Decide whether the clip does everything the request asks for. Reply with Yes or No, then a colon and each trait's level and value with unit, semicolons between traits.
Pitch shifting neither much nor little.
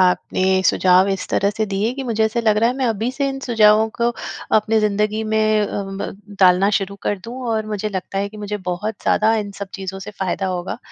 No: narrow, 2.1 semitones